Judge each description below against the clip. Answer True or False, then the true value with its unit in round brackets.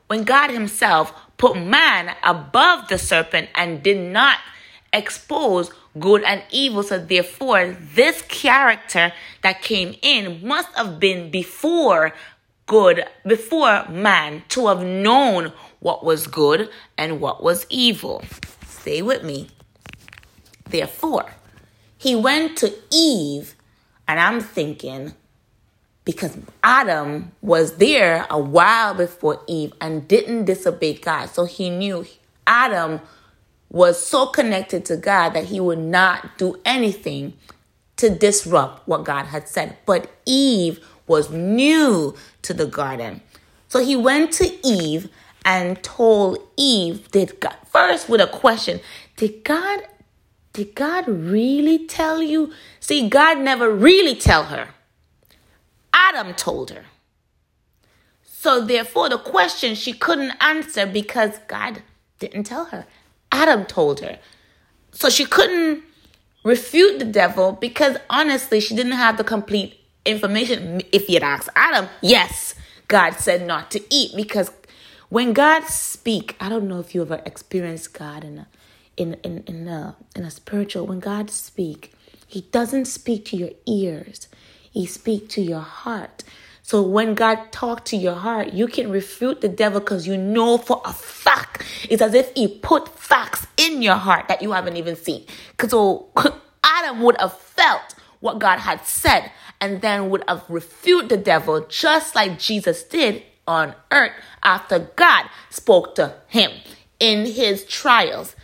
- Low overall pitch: False (210 Hz)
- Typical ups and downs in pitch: False (6.3 semitones)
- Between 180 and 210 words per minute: False (140 wpm)